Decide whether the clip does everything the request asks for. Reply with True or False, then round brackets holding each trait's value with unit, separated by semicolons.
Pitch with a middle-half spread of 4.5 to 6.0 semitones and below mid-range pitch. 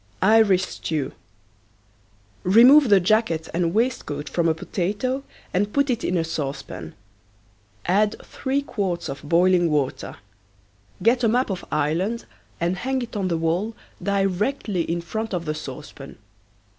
False (5.3 semitones; 185 Hz)